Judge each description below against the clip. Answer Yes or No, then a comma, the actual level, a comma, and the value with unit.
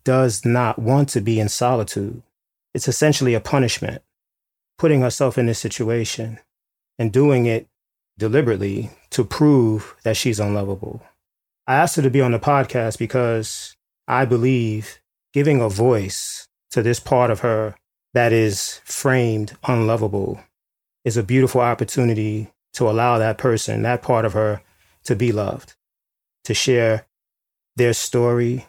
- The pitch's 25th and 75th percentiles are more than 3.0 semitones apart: No, narrow, 2.4 semitones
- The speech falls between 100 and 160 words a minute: Yes, average, 140 wpm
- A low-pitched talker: Yes, low, 115 Hz